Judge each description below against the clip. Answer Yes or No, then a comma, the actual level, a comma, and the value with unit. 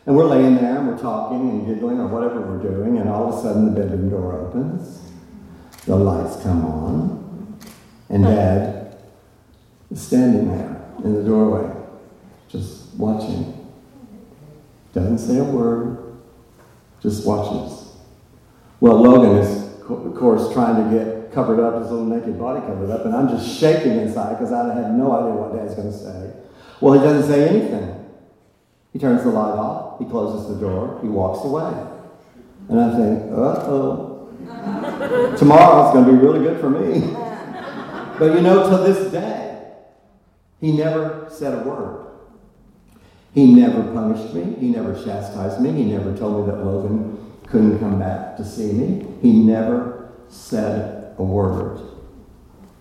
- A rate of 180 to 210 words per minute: No, average, 160 wpm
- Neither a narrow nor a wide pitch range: No, wide, 7.4 semitones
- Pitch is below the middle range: Yes, low, 115 Hz